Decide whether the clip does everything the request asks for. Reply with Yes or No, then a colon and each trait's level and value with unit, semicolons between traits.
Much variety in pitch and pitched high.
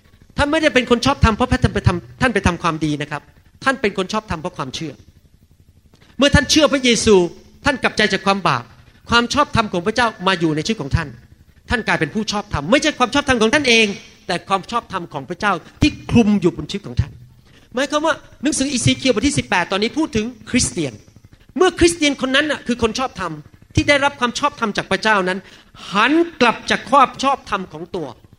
Yes: wide, 7.4 semitones; high, 215 Hz